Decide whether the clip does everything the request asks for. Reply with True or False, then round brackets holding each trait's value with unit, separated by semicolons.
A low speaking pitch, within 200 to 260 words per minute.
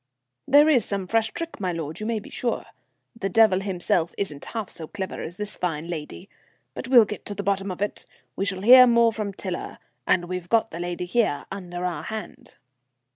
False (195 Hz; 205 wpm)